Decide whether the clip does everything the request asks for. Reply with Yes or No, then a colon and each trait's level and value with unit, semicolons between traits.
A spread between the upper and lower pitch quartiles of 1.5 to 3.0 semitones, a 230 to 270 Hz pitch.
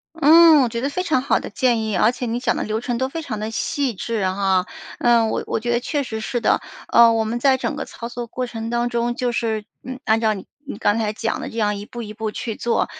Yes: narrow, 2.5 semitones; high, 235 Hz